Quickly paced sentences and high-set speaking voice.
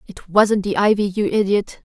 No: average, 190 wpm; high, 200 Hz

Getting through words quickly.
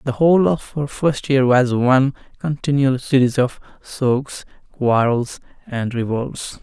No: slow, 135 wpm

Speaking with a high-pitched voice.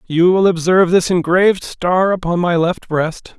No: medium, 175 Hz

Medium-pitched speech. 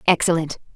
Yes: medium, 165 Hz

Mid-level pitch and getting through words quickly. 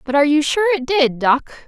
No: very high, 295 Hz; fast, 250 wpm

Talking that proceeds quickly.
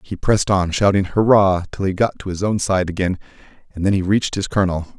Yes: fast, 230 wpm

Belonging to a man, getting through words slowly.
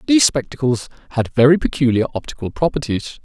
Yes: male; slow, 130 wpm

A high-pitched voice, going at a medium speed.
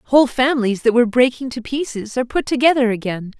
Yes: high, 245 Hz; average, 195 wpm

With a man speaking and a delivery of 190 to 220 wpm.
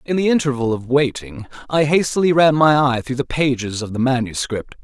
Yes: male; average, 200 wpm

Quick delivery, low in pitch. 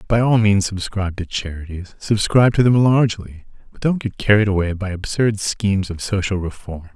No: average, 165 wpm; low, 100 Hz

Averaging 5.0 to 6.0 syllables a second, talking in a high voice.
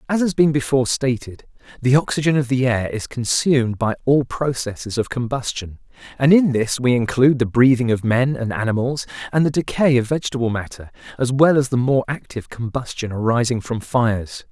No: 5.5 syllables/s; low, 125 Hz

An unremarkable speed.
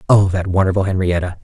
Yes: average, 170 wpm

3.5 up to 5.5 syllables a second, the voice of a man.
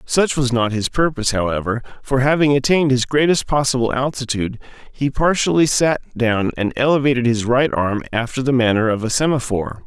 No: 5.7 syllables/s; male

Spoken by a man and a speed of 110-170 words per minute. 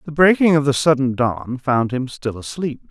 No: male; fast, 205 wpm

